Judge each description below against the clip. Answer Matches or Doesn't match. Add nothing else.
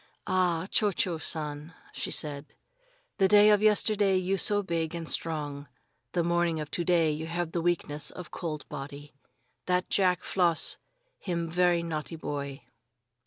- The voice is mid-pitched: Matches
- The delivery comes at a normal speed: Matches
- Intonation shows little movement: Doesn't match